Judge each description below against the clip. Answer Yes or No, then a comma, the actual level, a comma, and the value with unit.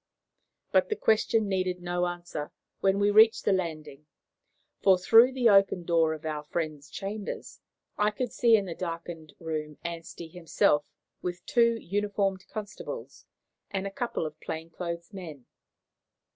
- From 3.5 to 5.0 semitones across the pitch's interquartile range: Yes, average, 4.0 semitones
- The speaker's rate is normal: Yes, average, 145 wpm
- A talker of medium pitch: Yes, medium, 180 Hz